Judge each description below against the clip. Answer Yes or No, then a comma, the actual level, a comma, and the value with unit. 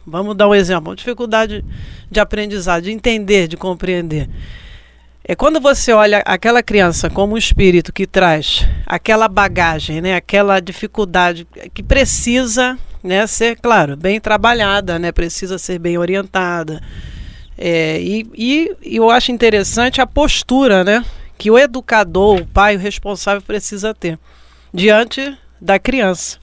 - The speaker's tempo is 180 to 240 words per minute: No, average, 140 wpm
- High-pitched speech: Yes, high, 200 Hz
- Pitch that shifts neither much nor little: Yes, average, 4.4 semitones